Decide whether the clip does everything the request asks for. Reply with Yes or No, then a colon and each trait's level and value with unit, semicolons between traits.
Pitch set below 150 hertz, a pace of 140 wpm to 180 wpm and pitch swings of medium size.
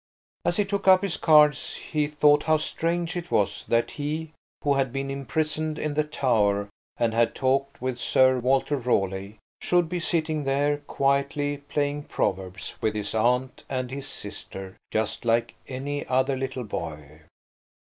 Yes: low, 135 Hz; average, 160 wpm; average, 4.2 semitones